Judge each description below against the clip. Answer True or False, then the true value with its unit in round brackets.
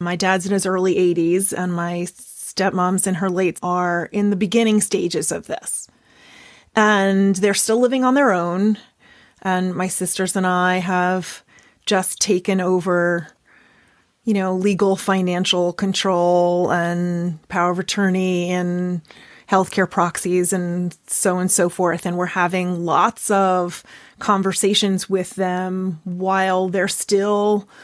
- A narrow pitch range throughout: True (1.7 semitones)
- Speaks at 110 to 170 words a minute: True (140 wpm)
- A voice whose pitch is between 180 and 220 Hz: True (185 Hz)